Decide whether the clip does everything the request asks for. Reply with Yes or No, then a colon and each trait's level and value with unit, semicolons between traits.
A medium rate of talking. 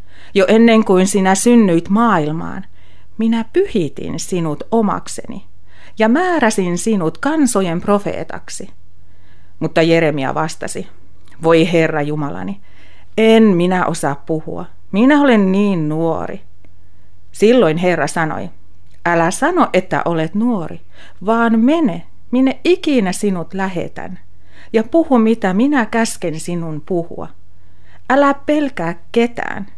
Yes: average, 105 wpm